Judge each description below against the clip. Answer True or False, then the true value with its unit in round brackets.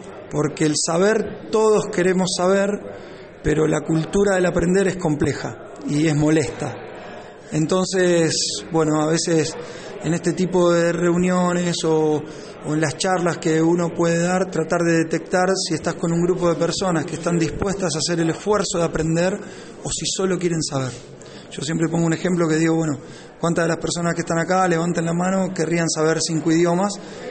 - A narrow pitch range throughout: True (2.3 semitones)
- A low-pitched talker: False (170 Hz)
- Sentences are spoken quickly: False (175 wpm)